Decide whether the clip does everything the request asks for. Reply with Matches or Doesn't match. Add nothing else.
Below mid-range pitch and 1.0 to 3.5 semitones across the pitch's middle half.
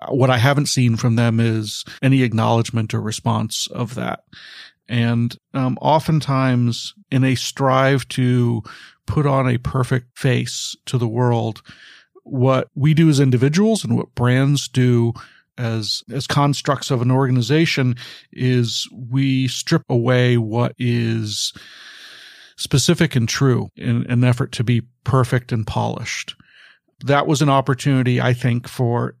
Matches